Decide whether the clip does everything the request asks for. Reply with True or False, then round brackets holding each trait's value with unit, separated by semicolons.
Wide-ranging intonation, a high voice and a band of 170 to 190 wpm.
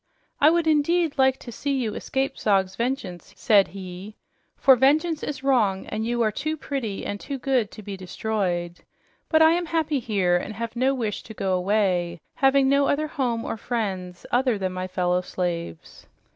True (6.3 semitones; 225 Hz; 185 wpm)